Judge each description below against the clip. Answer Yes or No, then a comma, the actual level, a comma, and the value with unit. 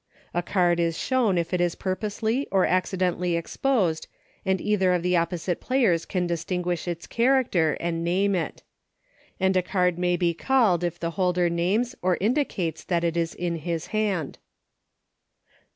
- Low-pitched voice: No, medium, 180 Hz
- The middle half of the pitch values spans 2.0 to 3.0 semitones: Yes, narrow, 2.5 semitones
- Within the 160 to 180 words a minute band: Yes, average, 170 wpm